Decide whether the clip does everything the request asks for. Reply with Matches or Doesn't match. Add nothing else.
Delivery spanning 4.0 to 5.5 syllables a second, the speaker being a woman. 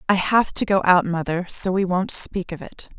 Matches